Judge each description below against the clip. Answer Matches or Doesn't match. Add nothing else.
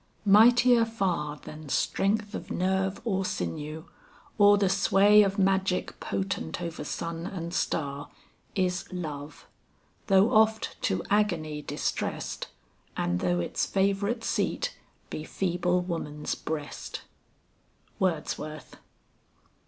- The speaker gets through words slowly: Matches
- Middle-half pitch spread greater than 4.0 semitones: Matches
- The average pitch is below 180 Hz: Doesn't match